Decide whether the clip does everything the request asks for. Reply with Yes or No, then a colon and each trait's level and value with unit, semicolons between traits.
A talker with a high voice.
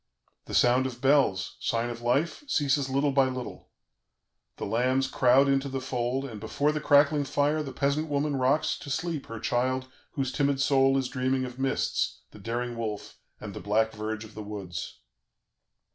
No: low, 130 Hz